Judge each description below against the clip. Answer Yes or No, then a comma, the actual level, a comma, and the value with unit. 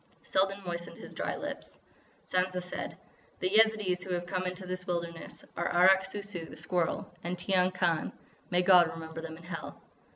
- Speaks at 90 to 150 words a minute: No, average, 175 wpm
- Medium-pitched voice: Yes, medium, 180 Hz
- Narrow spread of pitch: Yes, narrow, 1.5 semitones